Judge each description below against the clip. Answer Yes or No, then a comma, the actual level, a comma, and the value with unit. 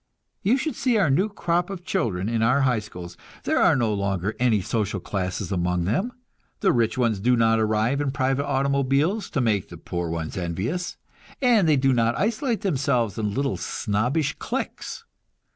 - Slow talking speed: No, average, 175 wpm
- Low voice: Yes, low, 125 Hz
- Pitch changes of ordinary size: No, wide, 6.4 semitones